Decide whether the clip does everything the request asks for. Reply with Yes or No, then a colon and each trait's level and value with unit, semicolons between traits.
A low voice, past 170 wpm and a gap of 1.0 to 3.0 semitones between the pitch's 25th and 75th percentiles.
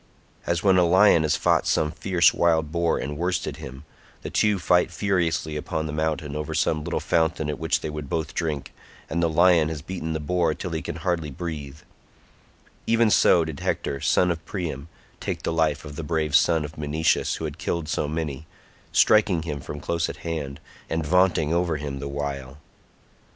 Yes: very low, 80 Hz; average, 190 wpm; narrow, 2.4 semitones